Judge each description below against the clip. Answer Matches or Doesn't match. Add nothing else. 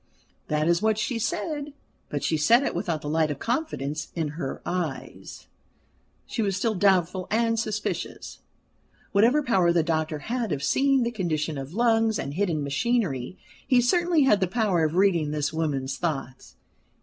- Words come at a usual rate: Matches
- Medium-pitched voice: Matches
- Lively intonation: Matches